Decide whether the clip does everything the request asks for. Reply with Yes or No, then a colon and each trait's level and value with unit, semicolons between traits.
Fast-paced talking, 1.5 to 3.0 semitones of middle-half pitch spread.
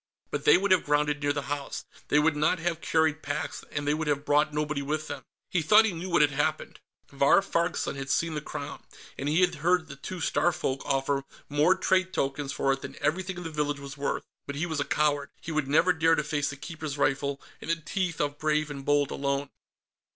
Yes: fast, 230 wpm; narrow, 2.4 semitones